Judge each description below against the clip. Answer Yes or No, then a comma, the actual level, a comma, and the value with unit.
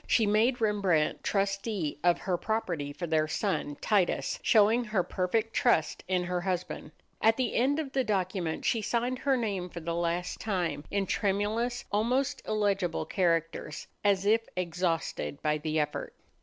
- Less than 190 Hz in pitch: No, high, 195 Hz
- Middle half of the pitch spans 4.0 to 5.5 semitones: Yes, average, 4.4 semitones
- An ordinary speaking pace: Yes, average, 155 wpm